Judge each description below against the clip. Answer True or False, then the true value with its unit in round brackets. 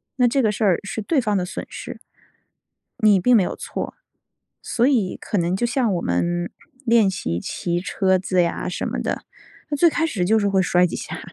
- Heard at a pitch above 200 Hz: False (195 Hz)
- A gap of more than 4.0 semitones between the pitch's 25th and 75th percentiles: True (4.6 semitones)